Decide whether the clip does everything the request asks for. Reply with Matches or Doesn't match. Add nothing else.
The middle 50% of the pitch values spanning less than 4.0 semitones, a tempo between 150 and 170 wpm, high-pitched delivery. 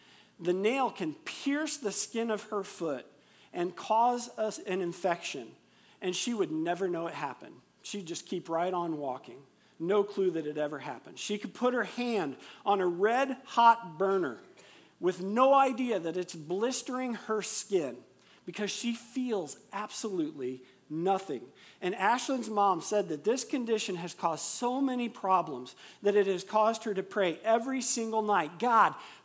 Doesn't match